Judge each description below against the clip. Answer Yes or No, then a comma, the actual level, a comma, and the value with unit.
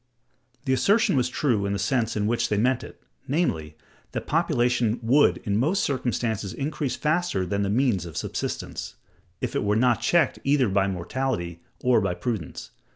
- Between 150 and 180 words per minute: Yes, average, 170 wpm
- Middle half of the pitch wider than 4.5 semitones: Yes, average, 4.9 semitones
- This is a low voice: Yes, low, 120 Hz